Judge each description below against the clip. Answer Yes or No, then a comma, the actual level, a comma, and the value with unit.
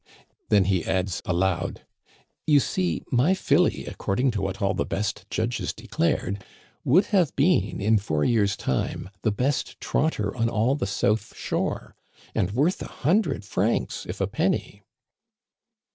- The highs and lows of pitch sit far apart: Yes, wide, 6.5 semitones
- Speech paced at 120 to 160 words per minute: Yes, average, 150 wpm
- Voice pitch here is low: Yes, low, 110 Hz